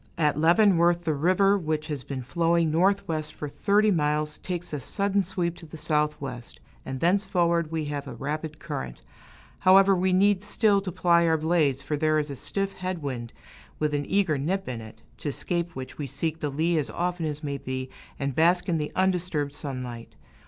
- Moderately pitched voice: Yes, medium, 160 Hz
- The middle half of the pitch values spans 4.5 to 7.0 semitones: No, average, 3.8 semitones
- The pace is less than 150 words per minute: No, average, 190 wpm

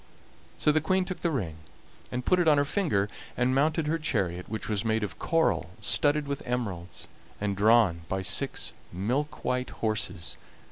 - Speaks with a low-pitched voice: Yes, low, 125 Hz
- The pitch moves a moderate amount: No, wide, 7.2 semitones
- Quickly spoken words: No, average, 175 wpm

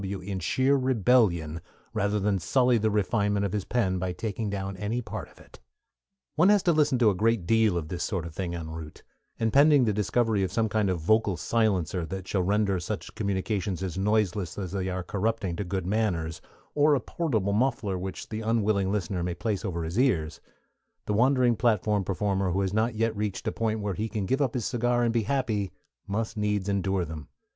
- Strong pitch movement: No, average, 3.3 semitones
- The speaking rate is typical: No, fast, 210 wpm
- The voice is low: Yes, low, 105 Hz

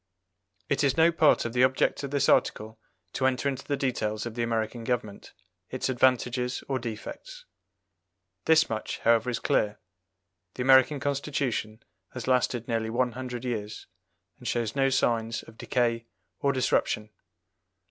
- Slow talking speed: No, average, 150 wpm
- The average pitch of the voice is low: Yes, low, 125 Hz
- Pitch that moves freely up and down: No, average, 2.7 semitones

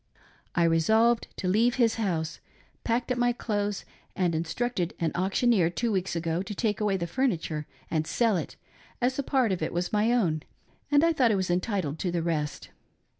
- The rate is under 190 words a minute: No, average, 195 wpm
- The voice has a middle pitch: No, high, 195 Hz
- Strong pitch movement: Yes, wide, 5.7 semitones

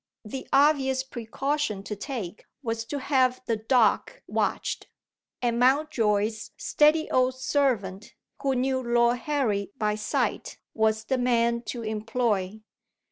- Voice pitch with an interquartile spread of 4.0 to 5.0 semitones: No, average, 3.5 semitones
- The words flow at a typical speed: No, slow, 125 wpm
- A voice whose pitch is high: Yes, high, 240 Hz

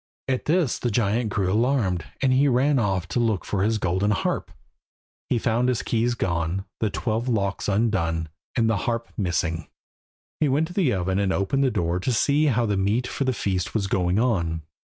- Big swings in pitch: No, average, 4.7 semitones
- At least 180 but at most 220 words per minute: Yes, average, 200 wpm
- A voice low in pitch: Yes, low, 110 Hz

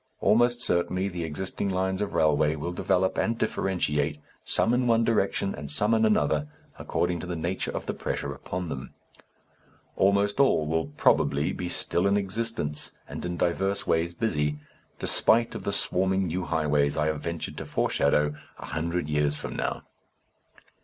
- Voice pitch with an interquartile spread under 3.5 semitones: No, average, 4.5 semitones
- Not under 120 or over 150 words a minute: No, average, 165 wpm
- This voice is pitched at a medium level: No, very low, 90 Hz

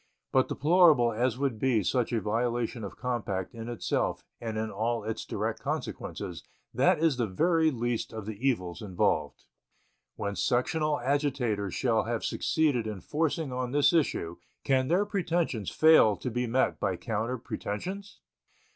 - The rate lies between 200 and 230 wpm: No, average, 155 wpm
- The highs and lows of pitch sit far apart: No, average, 4.8 semitones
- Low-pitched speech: Yes, low, 120 Hz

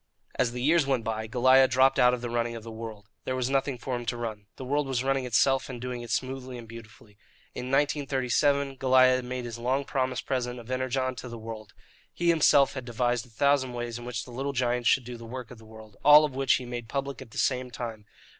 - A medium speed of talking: No, fast, 240 wpm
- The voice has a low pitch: Yes, low, 125 Hz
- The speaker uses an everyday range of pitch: No, narrow, 2.1 semitones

